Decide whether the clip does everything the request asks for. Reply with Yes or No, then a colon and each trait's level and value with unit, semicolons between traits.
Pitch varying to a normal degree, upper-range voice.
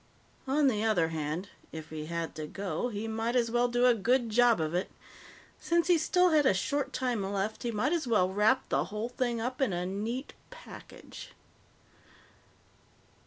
Yes: average, 4.9 semitones; high, 225 Hz